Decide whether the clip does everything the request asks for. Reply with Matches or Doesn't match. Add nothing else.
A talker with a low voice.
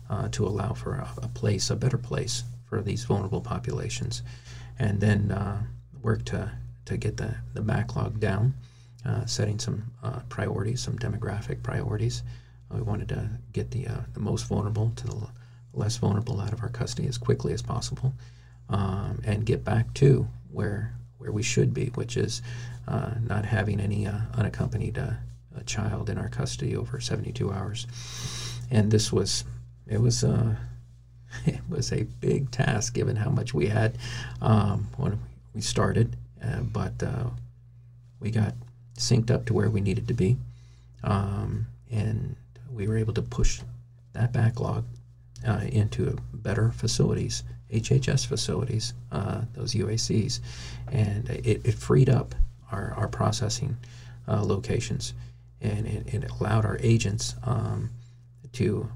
Matches